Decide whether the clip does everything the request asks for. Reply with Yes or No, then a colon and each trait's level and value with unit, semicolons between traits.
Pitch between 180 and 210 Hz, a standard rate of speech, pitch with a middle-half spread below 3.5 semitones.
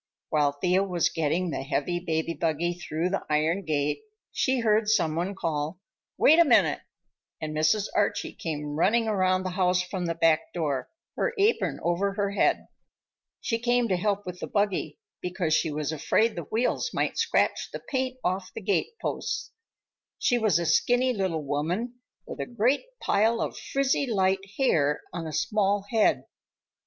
No: medium, 185 Hz; average, 170 wpm; wide, 5.4 semitones